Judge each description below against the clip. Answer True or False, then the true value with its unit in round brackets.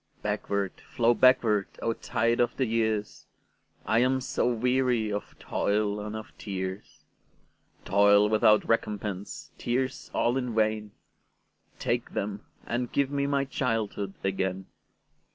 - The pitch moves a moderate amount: True (3.1 semitones)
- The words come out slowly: True (115 wpm)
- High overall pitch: False (110 Hz)